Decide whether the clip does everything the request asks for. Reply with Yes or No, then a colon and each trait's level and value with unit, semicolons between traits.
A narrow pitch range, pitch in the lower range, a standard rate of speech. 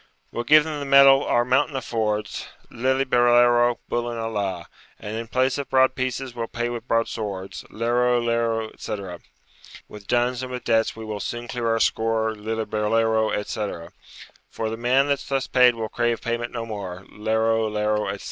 Yes: narrow, 2.0 semitones; low, 115 Hz; average, 170 wpm